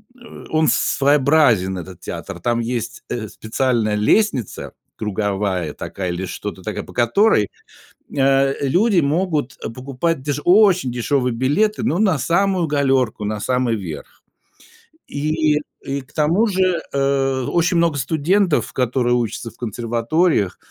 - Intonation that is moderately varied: No, wide, 5.9 semitones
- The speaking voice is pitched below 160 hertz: Yes, low, 135 Hz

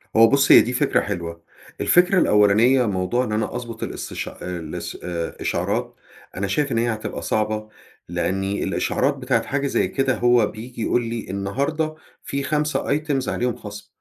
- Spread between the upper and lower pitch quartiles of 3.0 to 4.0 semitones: No, average, 4.7 semitones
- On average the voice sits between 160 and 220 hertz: No, low, 115 Hz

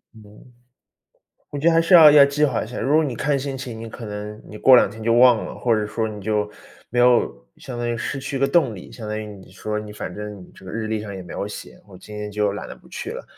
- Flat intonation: No, average, 4.2 semitones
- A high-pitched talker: No, low, 110 Hz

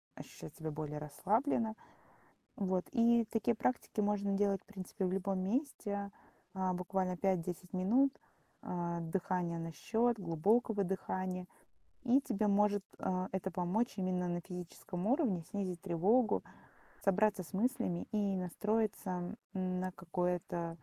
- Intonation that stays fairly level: No, average, 3.0 semitones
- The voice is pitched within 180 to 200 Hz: Yes, high, 190 Hz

